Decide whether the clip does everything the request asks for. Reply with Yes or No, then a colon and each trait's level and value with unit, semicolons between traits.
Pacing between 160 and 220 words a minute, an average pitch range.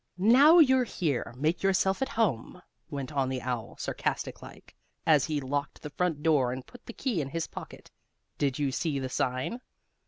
No: average, 185 wpm; wide, 6.6 semitones